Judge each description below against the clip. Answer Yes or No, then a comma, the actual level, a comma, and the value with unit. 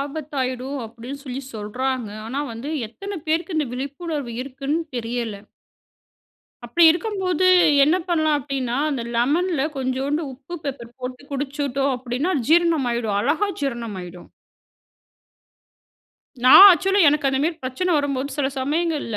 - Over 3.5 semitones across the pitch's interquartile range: Yes, average, 3.9 semitones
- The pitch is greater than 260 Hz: Yes, very high, 275 Hz